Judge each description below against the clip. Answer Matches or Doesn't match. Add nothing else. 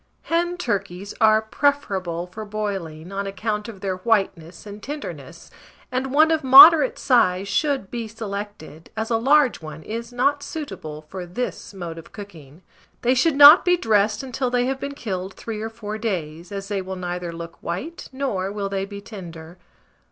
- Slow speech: Doesn't match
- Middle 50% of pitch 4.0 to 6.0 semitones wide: Matches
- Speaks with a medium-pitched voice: Doesn't match